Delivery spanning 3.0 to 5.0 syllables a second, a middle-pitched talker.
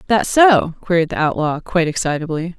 No: 5.5 syllables/s; medium, 175 Hz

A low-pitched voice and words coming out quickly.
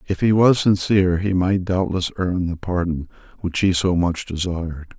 No: very low, 90 Hz; average, 180 wpm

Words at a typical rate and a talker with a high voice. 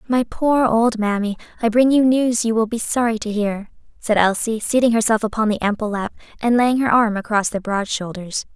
No: fast, 210 wpm; high, 225 Hz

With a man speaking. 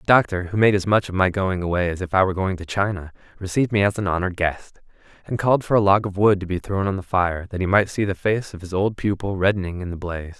Yes: male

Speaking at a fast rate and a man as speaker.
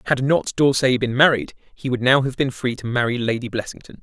Yes: fast, 225 wpm; male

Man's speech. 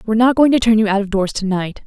No: female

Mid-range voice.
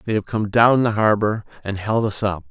No: low, 105 Hz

